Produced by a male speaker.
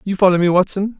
Yes: male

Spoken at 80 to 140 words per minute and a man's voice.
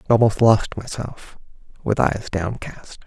Yes: slow, 135 wpm; male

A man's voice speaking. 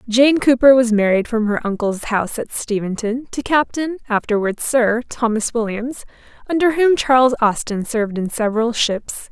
No: female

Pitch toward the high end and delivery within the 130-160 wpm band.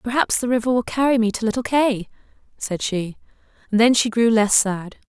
No: high, 230 Hz; average, 200 wpm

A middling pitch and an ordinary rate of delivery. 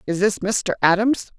No: high, 200 Hz; average, 175 wpm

